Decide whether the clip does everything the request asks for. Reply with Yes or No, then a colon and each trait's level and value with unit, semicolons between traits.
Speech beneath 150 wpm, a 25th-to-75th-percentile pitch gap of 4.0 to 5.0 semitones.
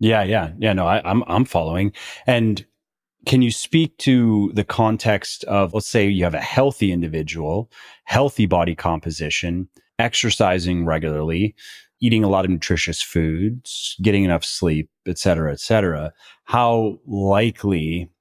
Yes: average, 140 wpm; average, 4.6 semitones